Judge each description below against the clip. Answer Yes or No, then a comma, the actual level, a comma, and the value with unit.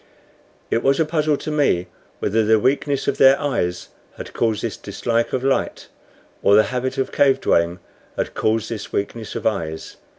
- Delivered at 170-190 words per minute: Yes, average, 175 wpm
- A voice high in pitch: No, low, 115 Hz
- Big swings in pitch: No, average, 4.5 semitones